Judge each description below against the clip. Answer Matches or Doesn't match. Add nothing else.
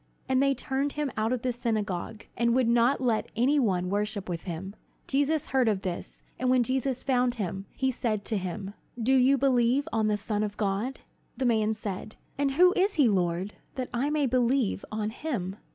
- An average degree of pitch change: Matches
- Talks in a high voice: Matches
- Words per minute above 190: Matches